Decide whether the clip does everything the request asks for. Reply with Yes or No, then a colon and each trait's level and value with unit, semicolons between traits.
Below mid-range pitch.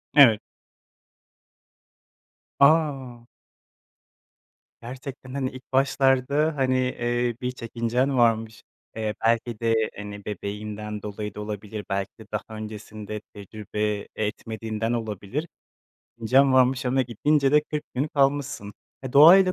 Yes: low, 120 Hz